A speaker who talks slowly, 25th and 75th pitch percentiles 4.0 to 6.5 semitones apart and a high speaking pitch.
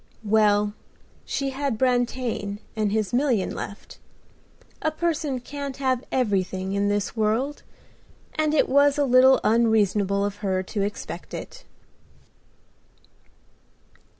Yes: slow, 115 wpm; average, 4.9 semitones; high, 230 Hz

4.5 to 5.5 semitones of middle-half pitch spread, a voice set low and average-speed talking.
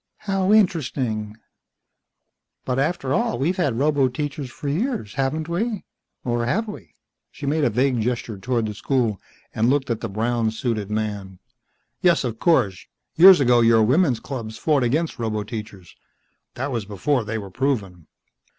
Yes: average, 5.2 semitones; low, 125 Hz; average, 155 wpm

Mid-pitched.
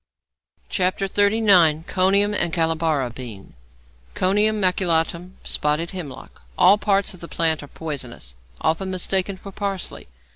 Yes: medium, 180 Hz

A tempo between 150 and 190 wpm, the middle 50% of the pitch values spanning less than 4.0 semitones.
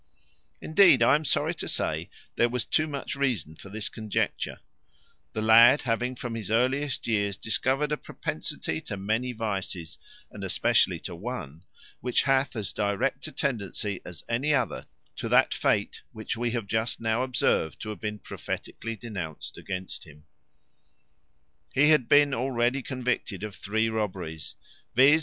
No: average, 155 wpm; average, 4.3 semitones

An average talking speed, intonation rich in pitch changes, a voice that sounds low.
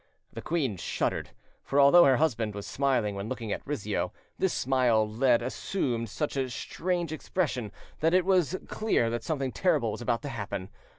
Yes: average, 175 wpm; wide, 5.8 semitones; low, 130 Hz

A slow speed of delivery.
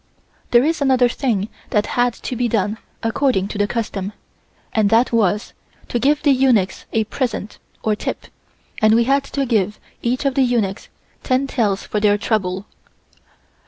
No: average, 165 wpm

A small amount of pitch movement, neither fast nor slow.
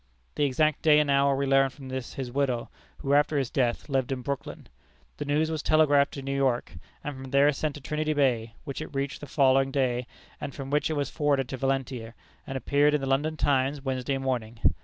No: narrow, 1.7 semitones; fast, 215 wpm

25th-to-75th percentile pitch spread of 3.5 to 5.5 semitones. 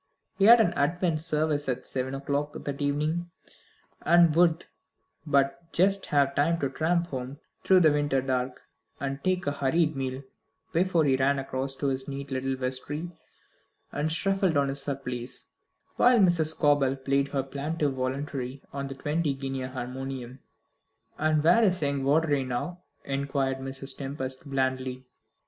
No: average, 3.1 semitones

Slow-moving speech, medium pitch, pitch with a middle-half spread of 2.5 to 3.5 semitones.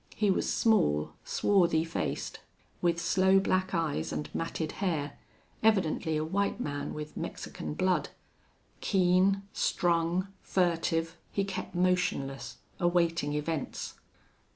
Yes: slow, 110 wpm; medium, 170 Hz; average, 3.0 semitones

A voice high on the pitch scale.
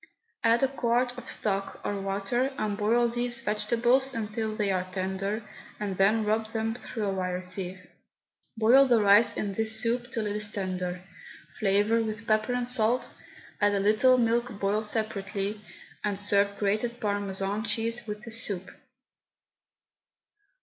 Yes: high, 215 Hz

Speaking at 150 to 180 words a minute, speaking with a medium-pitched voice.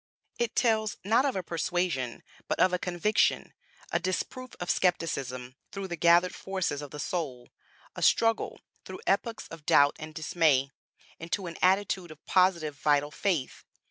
Yes: average, 155 wpm; medium, 175 Hz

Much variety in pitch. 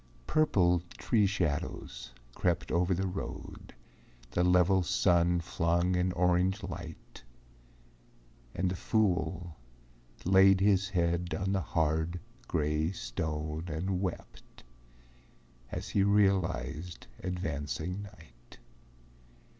No: average, 2.7 semitones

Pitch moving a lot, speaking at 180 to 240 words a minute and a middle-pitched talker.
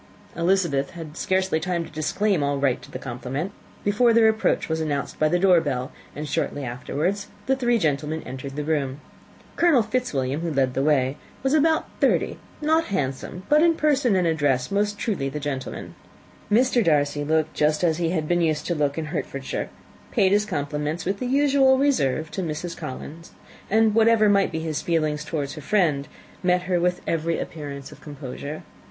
Yes: wide, 6.0 semitones; average, 185 wpm; medium, 160 Hz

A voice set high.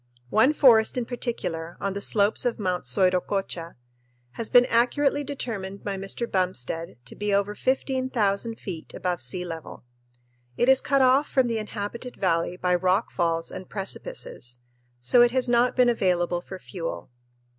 Yes: high, 200 Hz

